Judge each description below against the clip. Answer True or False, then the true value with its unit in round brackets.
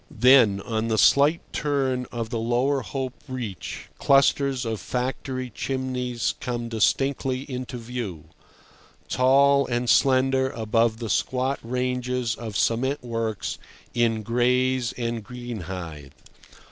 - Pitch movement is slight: True (2.3 semitones)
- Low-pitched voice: True (125 Hz)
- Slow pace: True (115 wpm)